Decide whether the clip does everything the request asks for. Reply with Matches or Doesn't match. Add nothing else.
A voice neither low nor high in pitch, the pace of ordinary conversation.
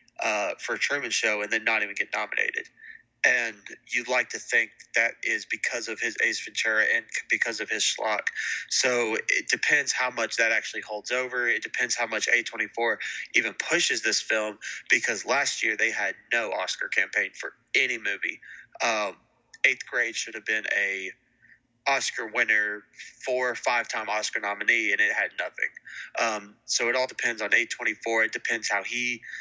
Doesn't match